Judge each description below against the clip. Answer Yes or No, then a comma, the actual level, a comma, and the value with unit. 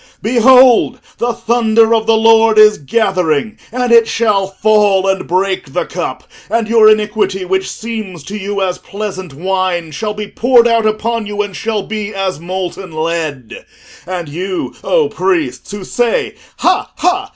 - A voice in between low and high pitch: No, high, 210 Hz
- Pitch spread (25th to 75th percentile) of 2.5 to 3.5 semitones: Yes, average, 3.2 semitones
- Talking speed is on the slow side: No, average, 160 wpm